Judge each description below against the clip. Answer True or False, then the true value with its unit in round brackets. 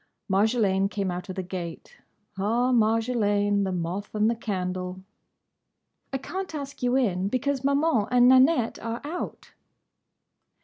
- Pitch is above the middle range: True (220 Hz)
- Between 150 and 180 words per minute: False (135 wpm)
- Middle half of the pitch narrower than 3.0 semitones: False (4.9 semitones)